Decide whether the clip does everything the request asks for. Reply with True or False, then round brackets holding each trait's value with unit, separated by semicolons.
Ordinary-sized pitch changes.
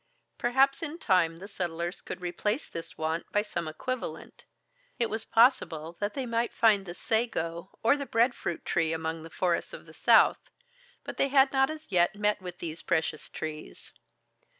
False (6.3 semitones)